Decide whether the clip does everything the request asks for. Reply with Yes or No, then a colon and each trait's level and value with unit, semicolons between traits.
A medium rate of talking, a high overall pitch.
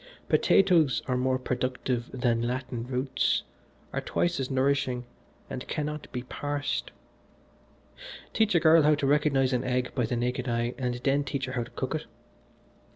No: average, 160 wpm; low, 130 Hz